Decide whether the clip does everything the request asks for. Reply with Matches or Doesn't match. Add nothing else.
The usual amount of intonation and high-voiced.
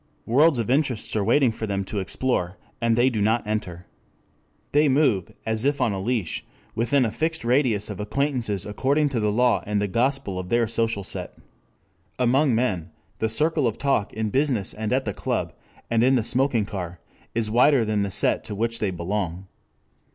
Doesn't match